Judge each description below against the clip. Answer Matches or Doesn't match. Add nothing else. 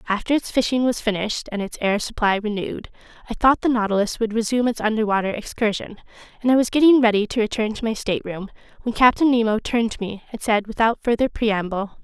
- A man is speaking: Doesn't match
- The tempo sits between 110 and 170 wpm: Doesn't match